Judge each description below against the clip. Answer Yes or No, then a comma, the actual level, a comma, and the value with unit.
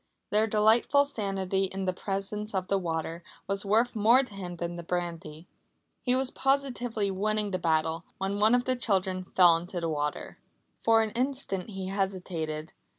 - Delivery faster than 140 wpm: Yes, average, 170 wpm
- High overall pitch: Yes, high, 195 Hz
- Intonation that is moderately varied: Yes, average, 3.8 semitones